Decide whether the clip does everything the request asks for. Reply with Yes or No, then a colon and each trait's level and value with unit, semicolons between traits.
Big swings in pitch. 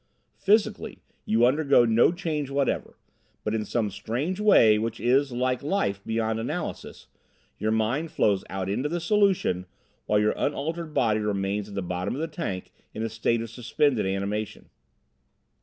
Yes: wide, 6.0 semitones